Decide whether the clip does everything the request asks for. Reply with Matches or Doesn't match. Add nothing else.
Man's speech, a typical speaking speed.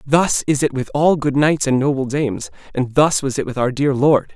Doesn't match